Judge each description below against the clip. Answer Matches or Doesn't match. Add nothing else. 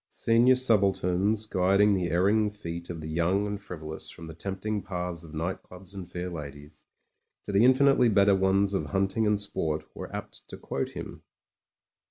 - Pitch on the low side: Matches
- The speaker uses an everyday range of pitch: Matches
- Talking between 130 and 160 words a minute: Doesn't match